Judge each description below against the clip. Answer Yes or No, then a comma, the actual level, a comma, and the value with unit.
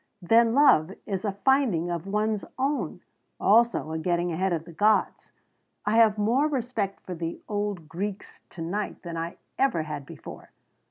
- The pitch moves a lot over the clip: No, average, 4.9 semitones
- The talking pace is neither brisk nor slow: Yes, average, 165 wpm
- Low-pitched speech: No, high, 200 Hz